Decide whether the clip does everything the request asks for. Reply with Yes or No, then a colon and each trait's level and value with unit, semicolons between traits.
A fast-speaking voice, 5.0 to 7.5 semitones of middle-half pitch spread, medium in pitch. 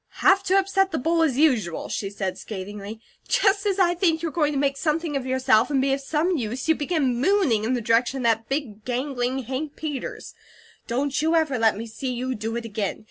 No: fast, 220 wpm; wide, 5.6 semitones; very high, 270 Hz